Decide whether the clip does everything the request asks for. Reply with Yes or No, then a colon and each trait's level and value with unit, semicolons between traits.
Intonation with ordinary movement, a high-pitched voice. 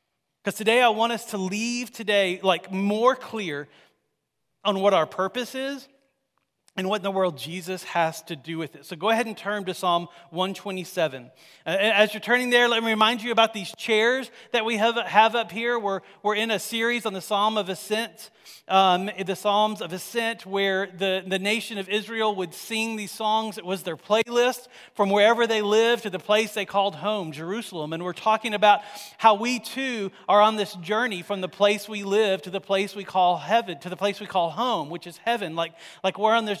Yes: average, 3.0 semitones; high, 205 Hz